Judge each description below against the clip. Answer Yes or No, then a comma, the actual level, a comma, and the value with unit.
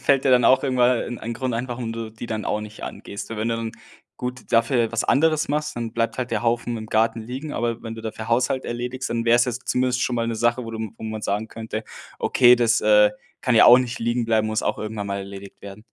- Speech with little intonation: Yes, narrow, 2.0 semitones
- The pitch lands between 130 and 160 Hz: No, low, 115 Hz